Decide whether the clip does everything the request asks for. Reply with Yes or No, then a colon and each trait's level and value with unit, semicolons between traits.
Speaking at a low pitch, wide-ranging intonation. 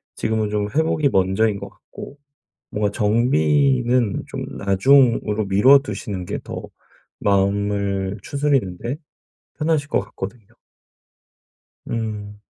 No: low, 105 Hz; average, 4.6 semitones